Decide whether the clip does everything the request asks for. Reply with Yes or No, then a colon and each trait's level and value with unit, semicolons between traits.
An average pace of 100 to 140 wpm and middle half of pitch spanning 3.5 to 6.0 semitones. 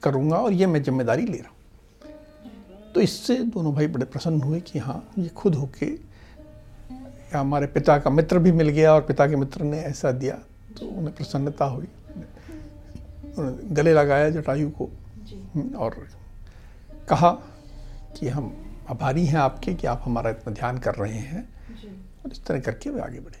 No: average, 165 wpm; average, 5.2 semitones